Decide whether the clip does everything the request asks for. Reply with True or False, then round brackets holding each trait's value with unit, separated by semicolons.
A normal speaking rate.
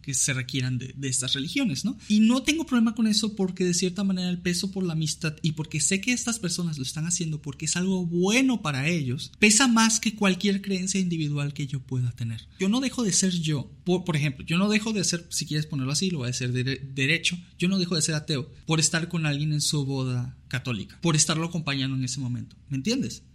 False (245 wpm)